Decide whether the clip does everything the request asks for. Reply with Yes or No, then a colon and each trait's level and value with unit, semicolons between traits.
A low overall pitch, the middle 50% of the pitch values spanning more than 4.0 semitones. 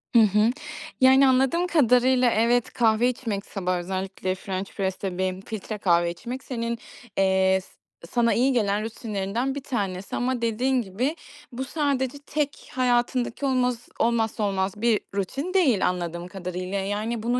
No: high, 230 Hz; average, 4.7 semitones